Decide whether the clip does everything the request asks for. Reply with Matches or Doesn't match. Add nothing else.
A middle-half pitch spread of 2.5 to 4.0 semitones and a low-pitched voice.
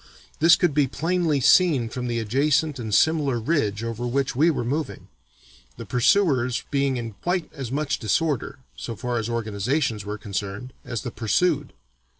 Doesn't match